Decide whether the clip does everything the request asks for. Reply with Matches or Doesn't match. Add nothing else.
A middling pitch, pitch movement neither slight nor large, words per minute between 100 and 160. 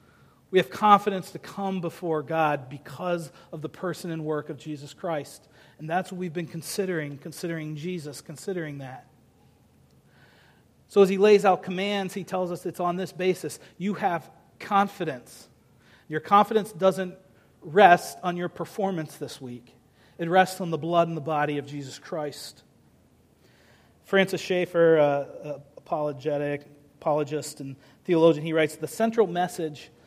Matches